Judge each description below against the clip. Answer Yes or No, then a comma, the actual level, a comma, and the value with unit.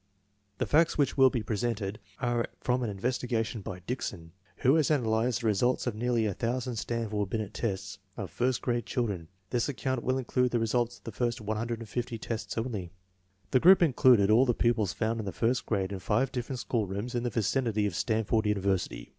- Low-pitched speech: Yes, low, 115 Hz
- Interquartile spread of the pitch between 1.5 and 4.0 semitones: Yes, average, 2.9 semitones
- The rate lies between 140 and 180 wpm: No, average, 195 wpm